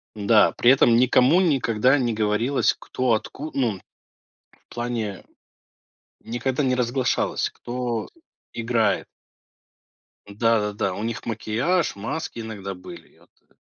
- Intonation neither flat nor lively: Yes, average, 3.0 semitones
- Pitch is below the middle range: Yes, low, 115 Hz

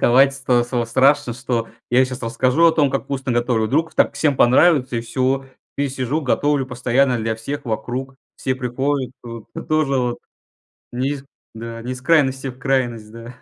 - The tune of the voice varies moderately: No, narrow, 2.3 semitones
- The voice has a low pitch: Yes, low, 130 Hz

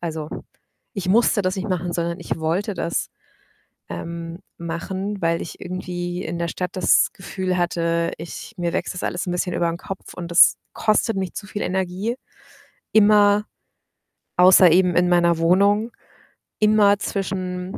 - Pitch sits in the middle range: Yes, medium, 180 Hz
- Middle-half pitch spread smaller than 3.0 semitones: Yes, narrow, 2.4 semitones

